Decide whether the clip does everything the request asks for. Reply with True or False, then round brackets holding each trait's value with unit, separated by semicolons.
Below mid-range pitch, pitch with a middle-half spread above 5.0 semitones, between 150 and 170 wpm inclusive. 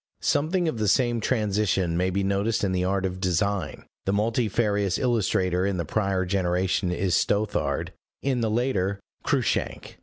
False (100 Hz; 3.2 semitones; 155 wpm)